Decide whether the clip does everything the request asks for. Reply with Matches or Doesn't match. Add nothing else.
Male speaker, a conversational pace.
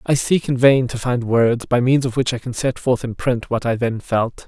Doesn't match